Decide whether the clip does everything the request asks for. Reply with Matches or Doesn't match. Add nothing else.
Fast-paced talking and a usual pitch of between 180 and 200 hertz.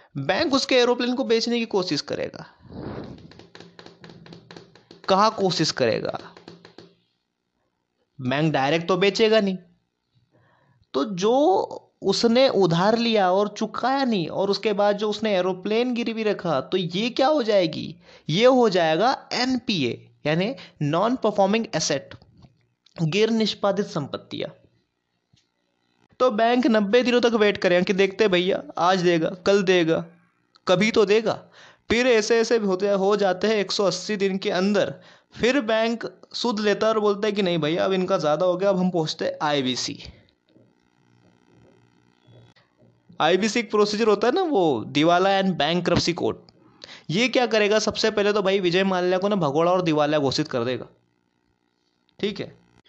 Doesn't match